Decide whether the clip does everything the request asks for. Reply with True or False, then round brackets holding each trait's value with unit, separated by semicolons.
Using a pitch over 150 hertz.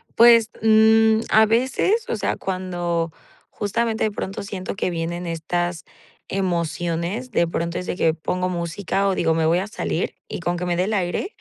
True (185 Hz)